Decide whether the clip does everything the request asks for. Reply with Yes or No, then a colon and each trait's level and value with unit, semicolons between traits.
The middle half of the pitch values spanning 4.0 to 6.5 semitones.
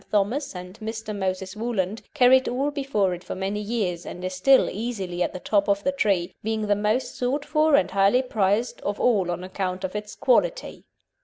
Yes: average, 4.8 semitones